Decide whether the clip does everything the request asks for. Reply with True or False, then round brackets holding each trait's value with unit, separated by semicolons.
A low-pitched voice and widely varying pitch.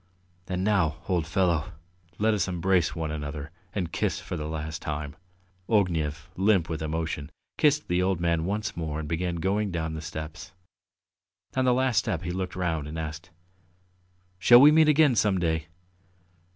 False (85 Hz; 3.7 semitones)